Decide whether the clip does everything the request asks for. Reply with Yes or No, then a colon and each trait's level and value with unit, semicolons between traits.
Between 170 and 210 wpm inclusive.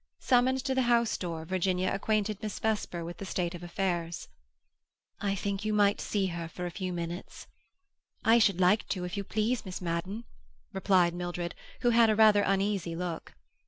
Yes: average, 180 wpm